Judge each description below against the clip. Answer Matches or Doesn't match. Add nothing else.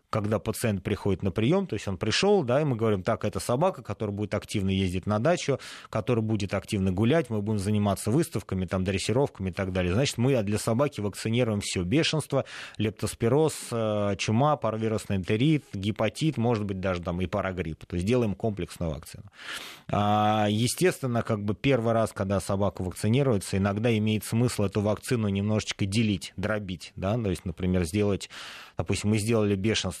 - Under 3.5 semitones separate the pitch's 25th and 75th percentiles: Matches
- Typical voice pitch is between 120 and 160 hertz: Doesn't match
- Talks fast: Matches